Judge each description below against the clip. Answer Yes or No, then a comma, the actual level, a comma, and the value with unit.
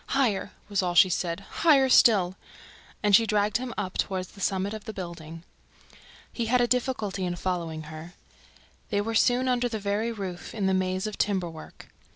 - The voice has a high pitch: Yes, high, 200 Hz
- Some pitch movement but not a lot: Yes, average, 3.8 semitones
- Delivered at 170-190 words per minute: Yes, average, 175 wpm